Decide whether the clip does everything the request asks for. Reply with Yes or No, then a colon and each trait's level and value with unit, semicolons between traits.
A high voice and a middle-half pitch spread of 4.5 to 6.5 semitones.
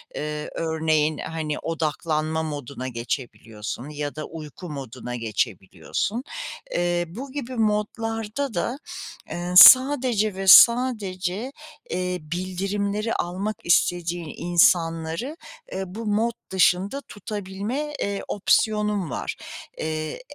No: medium, 180 Hz; average, 5.2 semitones